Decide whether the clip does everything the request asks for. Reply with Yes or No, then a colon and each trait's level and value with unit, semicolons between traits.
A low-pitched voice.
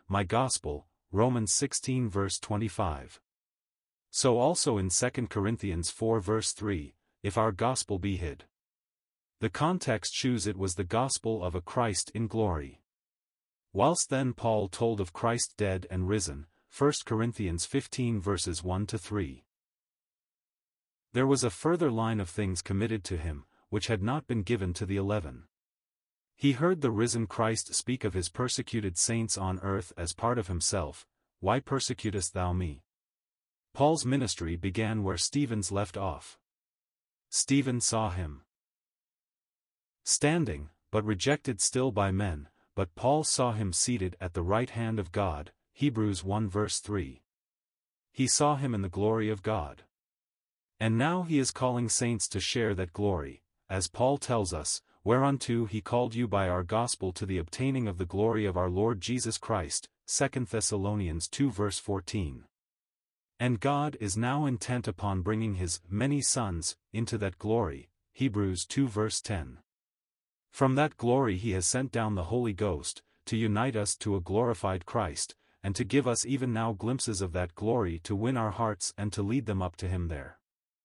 Yes: low, 105 Hz